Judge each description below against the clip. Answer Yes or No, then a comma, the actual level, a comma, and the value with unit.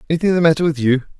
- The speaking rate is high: Yes, fast, 250 wpm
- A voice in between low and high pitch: Yes, medium, 155 Hz